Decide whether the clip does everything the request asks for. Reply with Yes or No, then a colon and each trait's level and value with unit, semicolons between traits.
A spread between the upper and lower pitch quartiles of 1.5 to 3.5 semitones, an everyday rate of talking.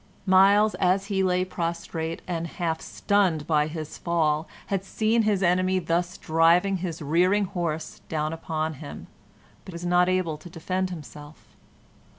Yes: narrow, 2.6 semitones; average, 150 wpm